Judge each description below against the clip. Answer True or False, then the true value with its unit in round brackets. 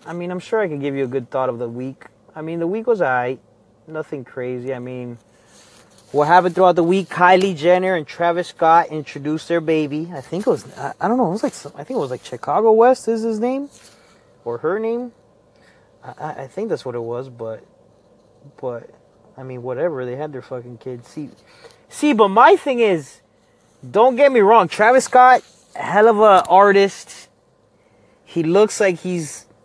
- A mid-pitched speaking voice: True (170 Hz)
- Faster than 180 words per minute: True (200 wpm)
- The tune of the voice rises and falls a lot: True (8.3 semitones)